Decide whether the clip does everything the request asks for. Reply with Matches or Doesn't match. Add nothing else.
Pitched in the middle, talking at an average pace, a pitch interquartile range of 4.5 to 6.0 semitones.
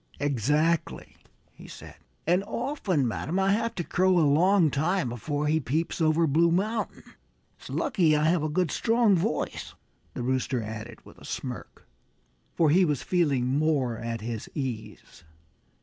Matches